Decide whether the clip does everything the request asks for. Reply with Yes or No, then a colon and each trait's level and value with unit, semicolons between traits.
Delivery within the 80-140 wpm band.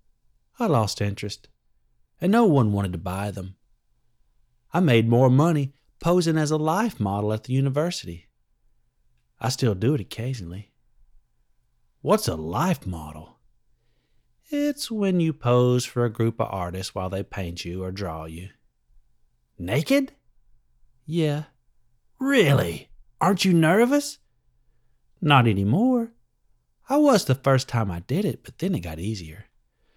Yes: slow, 135 wpm